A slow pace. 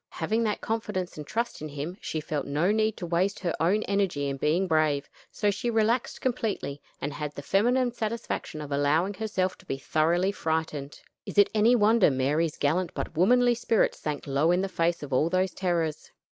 No: average, 195 wpm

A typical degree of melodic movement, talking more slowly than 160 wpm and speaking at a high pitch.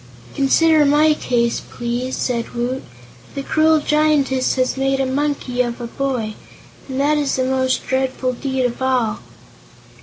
No: narrow, 2.3 semitones; average, 150 wpm; very high, 265 Hz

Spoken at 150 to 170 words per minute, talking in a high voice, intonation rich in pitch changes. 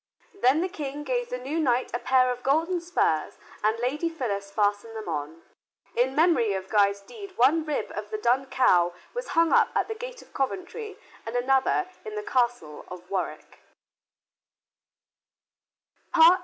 Yes: average, 160 wpm; very high, 255 Hz; wide, 7.6 semitones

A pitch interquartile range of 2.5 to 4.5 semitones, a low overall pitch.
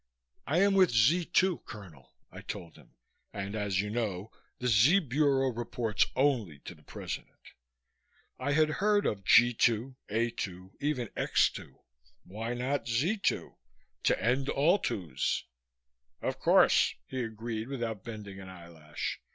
No: wide, 5.5 semitones; low, 115 Hz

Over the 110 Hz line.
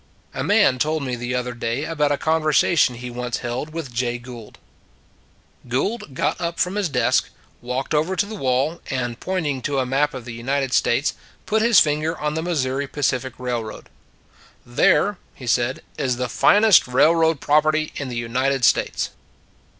Yes: low, 135 Hz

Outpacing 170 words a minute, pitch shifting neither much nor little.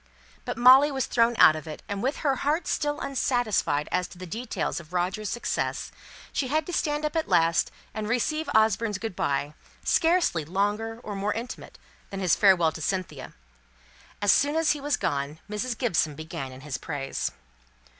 No: average, 180 wpm; wide, 7.9 semitones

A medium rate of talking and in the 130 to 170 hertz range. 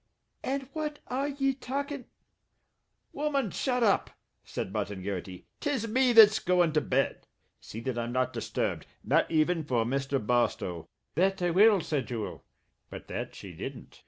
No: average, 160 wpm; medium, 180 Hz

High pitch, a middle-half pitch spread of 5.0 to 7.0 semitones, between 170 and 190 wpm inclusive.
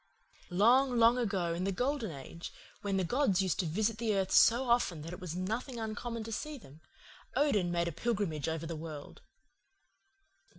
Yes: high, 200 Hz; wide, 5.6 semitones; average, 180 wpm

